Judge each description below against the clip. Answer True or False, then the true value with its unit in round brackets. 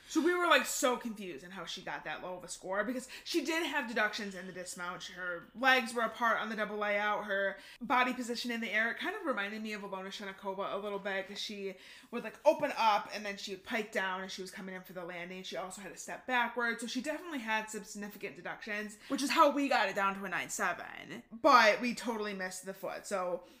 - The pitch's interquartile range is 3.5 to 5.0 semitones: True (4.5 semitones)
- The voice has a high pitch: True (210 Hz)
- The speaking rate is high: True (250 wpm)